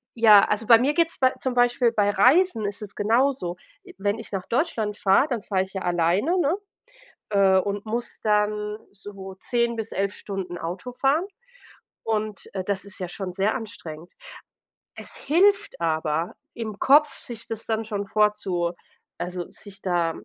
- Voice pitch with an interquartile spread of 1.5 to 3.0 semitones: No, average, 3.8 semitones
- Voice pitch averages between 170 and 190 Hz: No, high, 210 Hz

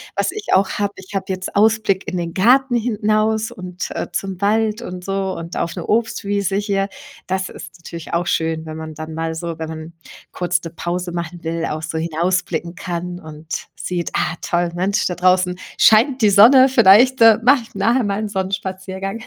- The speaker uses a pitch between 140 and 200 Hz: Yes, high, 190 Hz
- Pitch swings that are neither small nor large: Yes, average, 3.7 semitones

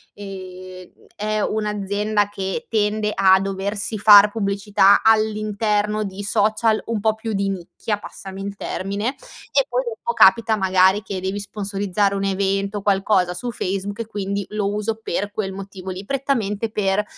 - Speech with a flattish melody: Yes, narrow, 1.6 semitones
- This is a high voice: Yes, high, 205 Hz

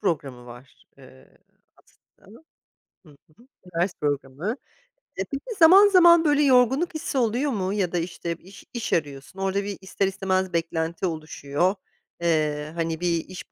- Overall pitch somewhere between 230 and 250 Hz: No, medium, 185 Hz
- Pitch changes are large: Yes, wide, 6.7 semitones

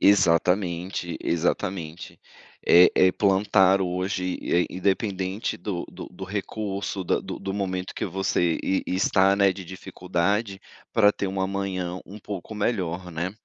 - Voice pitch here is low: Yes, very low, 95 Hz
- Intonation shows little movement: Yes, narrow, 1.6 semitones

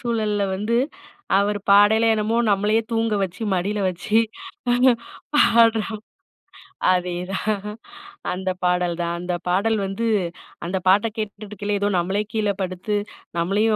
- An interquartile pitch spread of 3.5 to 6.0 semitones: No, average, 3.0 semitones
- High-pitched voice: Yes, high, 205 Hz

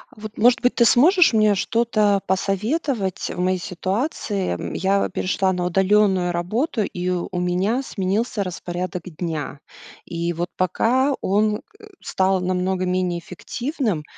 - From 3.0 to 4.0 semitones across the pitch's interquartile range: Yes, average, 3.3 semitones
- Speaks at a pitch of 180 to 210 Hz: Yes, high, 190 Hz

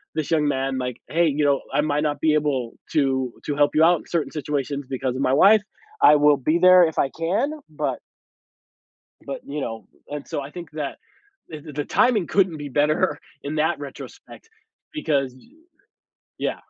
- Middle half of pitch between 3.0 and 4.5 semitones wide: No, narrow, 2.5 semitones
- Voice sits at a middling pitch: Yes, medium, 150 Hz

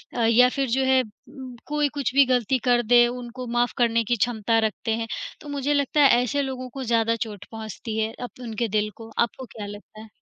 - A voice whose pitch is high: Yes, high, 240 Hz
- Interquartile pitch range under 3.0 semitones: Yes, narrow, 2.5 semitones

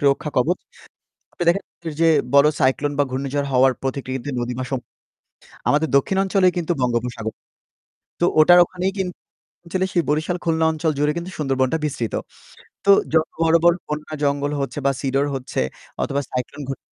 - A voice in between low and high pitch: Yes, medium, 145 Hz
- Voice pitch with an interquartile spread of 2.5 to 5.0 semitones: Yes, average, 4.1 semitones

